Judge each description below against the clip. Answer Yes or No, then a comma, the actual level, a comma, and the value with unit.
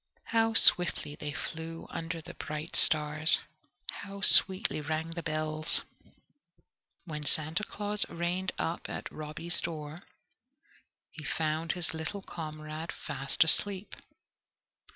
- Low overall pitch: No, medium, 160 Hz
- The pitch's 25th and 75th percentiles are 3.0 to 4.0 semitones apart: No, narrow, 2.4 semitones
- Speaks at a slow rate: Yes, slow, 110 wpm